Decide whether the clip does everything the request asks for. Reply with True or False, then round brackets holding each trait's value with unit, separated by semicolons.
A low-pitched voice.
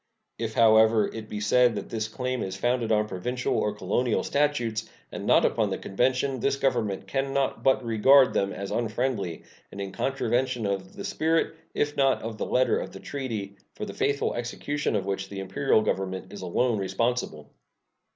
True (115 Hz)